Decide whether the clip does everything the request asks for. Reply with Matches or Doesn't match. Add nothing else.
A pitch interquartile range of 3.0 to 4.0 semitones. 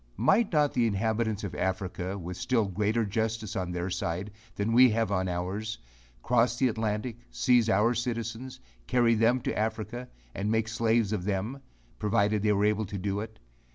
Doesn't match